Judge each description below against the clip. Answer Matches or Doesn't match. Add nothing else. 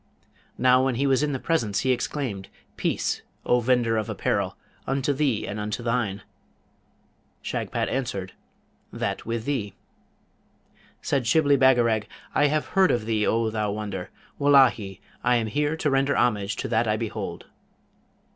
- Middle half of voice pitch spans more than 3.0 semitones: Matches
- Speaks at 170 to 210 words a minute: Doesn't match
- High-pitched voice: Doesn't match